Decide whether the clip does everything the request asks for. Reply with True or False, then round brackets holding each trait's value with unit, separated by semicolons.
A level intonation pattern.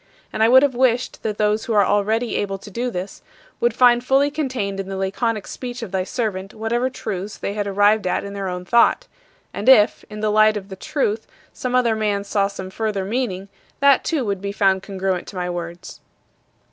False (3.5 semitones)